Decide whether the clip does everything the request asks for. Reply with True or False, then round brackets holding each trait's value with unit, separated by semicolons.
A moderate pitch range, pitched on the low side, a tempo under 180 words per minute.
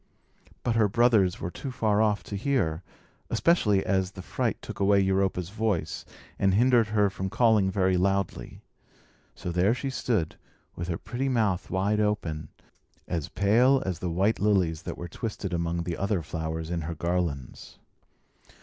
True (3.8 semitones; 95 Hz; 160 wpm)